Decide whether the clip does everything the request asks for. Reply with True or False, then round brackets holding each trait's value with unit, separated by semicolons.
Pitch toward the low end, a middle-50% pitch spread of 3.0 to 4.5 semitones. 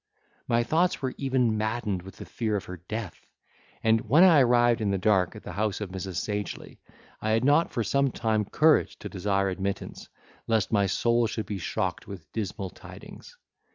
True (110 Hz; 3.5 semitones)